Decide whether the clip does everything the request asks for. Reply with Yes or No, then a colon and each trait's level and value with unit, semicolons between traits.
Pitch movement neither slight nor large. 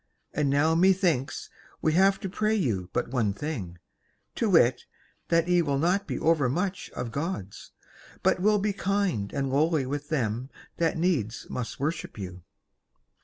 No: wide, 6.4 semitones